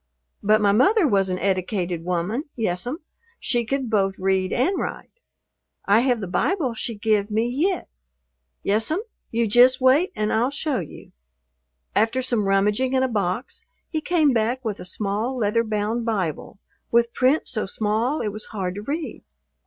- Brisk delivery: No, average, 165 wpm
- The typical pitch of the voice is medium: No, high, 225 Hz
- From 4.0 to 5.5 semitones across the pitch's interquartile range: Yes, average, 4.4 semitones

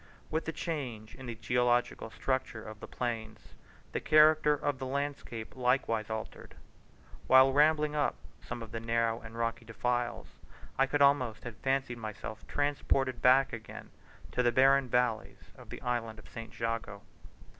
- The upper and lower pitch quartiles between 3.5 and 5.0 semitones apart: No, average, 3.1 semitones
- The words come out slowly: No, average, 155 wpm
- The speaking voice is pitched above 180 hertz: No, low, 125 Hz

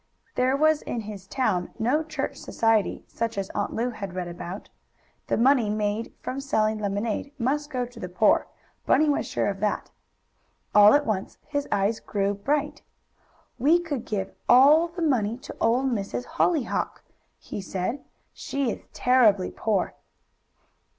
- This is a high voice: Yes, high, 230 Hz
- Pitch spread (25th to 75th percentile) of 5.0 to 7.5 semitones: Yes, average, 5.3 semitones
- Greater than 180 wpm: No, average, 155 wpm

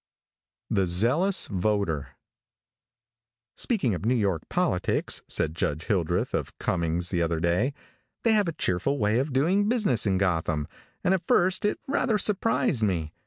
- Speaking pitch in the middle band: No, low, 105 Hz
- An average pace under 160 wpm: Yes, average, 150 wpm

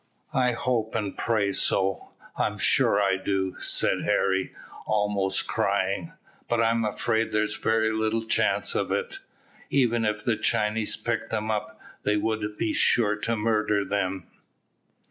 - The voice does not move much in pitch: Yes, narrow, 1.9 semitones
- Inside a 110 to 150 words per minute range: Yes, average, 145 wpm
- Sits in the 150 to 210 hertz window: No, low, 110 Hz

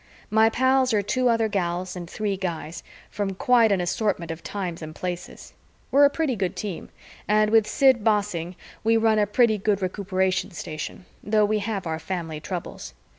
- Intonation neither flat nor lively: Yes, average, 3.7 semitones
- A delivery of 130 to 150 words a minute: No, average, 175 wpm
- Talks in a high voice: Yes, high, 200 Hz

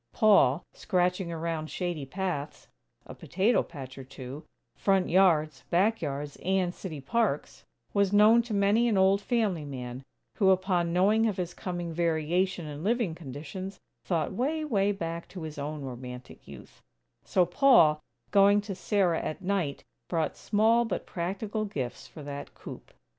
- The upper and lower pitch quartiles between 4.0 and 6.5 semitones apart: Yes, average, 4.7 semitones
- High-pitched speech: No, medium, 180 Hz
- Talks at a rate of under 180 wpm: Yes, average, 155 wpm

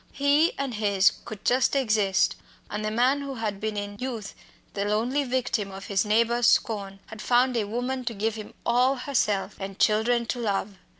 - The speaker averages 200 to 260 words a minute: No, average, 185 wpm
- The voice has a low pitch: No, high, 225 Hz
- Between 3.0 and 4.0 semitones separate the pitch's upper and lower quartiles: Yes, average, 3.4 semitones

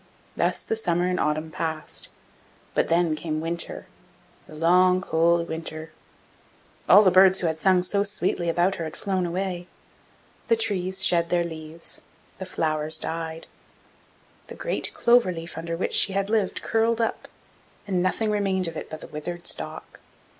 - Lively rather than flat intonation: No, average, 2.7 semitones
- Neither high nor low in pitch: Yes, medium, 175 Hz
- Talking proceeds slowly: No, average, 160 wpm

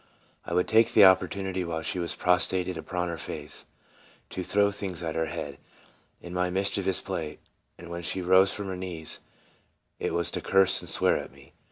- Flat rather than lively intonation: Yes, narrow, 2.1 semitones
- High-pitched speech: No, very low, 90 Hz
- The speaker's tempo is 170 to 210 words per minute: Yes, average, 190 wpm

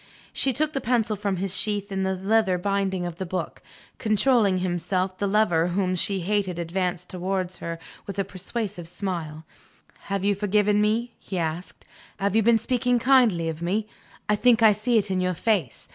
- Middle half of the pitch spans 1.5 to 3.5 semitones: Yes, average, 2.9 semitones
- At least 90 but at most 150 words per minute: No, average, 185 wpm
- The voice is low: No, high, 195 Hz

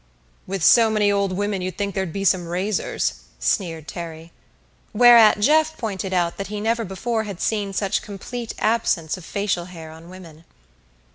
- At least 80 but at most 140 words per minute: No, average, 165 wpm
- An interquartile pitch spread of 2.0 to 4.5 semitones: Yes, average, 3.5 semitones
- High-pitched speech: Yes, high, 195 Hz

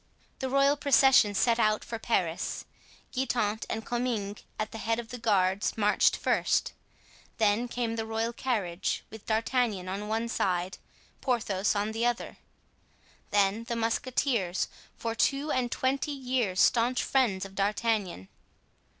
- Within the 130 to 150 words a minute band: Yes, average, 140 wpm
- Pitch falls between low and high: No, high, 225 Hz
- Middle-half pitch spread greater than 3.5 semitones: No, average, 3.2 semitones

